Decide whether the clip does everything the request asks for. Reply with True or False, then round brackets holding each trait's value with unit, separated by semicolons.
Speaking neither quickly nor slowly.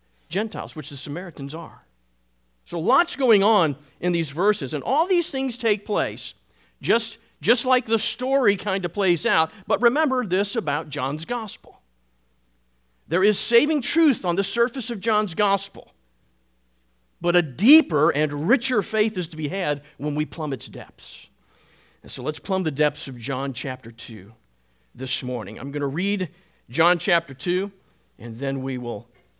True (165 wpm)